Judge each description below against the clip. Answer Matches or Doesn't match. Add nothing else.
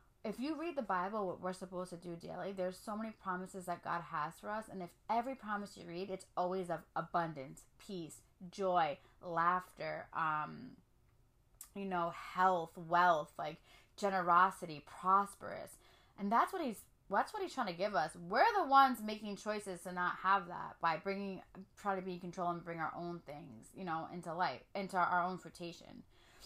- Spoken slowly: Doesn't match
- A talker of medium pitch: Matches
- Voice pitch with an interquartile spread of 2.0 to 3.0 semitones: Matches